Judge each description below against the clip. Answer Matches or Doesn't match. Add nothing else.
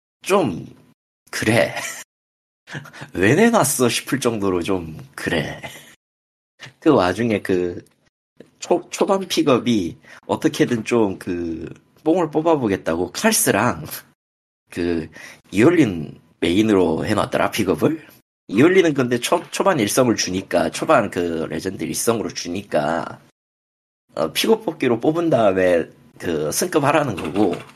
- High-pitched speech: Doesn't match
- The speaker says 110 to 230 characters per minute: Matches